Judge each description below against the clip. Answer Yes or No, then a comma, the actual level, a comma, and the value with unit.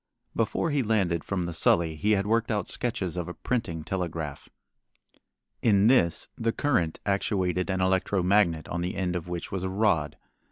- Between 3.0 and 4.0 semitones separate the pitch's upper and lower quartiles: Yes, average, 3.5 semitones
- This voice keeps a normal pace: Yes, average, 175 wpm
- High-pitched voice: No, very low, 95 Hz